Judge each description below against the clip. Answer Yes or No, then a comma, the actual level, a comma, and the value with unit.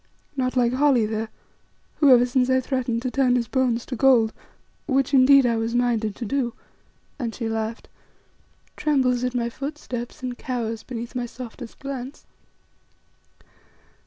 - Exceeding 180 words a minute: No, average, 150 wpm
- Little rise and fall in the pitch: Yes, narrow, 2.0 semitones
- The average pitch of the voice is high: Yes, high, 245 Hz